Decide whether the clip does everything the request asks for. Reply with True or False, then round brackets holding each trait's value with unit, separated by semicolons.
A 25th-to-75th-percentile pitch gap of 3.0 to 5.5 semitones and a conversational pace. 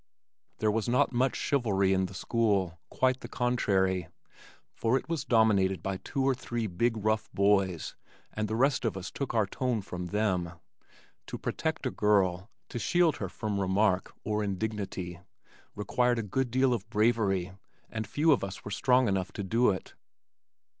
True (4.0 semitones; 170 wpm)